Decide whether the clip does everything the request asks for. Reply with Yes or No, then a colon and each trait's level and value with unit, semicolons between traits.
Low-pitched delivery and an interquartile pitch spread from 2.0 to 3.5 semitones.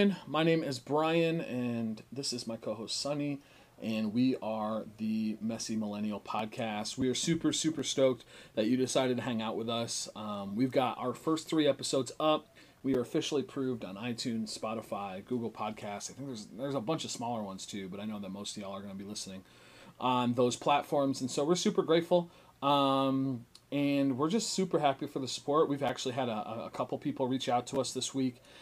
No: low, 130 Hz; average, 4.5 semitones